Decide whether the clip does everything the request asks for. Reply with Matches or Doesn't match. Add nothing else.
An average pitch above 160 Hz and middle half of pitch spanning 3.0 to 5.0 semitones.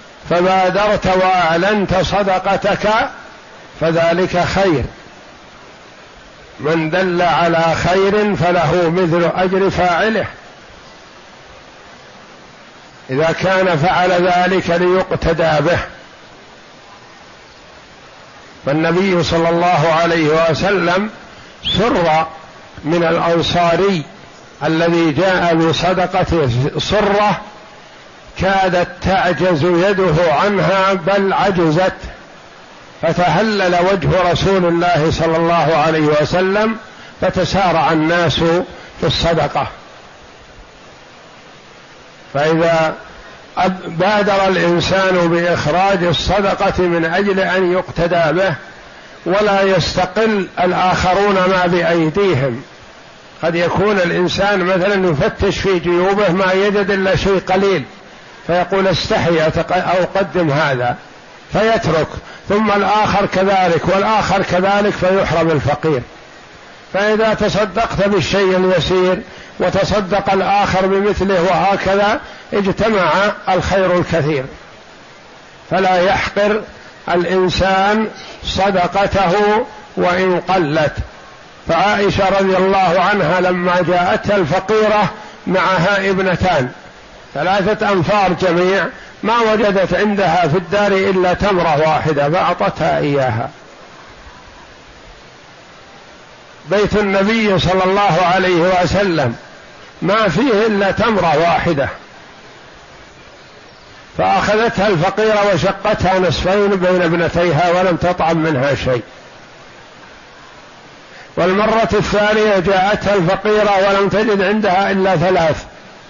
Doesn't match